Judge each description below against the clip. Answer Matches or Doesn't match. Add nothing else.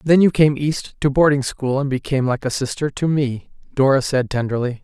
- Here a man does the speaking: Matches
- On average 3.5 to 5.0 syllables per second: Doesn't match